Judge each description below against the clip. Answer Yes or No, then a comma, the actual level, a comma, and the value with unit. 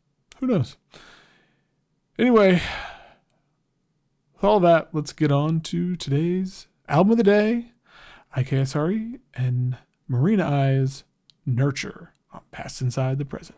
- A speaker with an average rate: No, slow, 110 wpm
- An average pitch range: No, wide, 6.1 semitones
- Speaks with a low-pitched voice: No, medium, 155 Hz